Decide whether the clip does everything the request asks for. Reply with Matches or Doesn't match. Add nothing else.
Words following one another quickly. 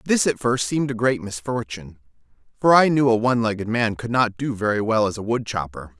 Matches